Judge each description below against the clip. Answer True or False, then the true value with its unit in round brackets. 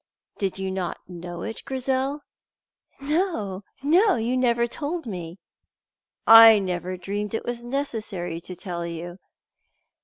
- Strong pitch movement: True (6.3 semitones)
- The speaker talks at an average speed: False (125 wpm)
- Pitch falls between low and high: False (220 Hz)